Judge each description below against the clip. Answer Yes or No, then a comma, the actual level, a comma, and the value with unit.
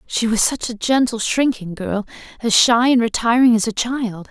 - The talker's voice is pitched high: Yes, high, 230 Hz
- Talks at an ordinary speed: Yes, average, 195 wpm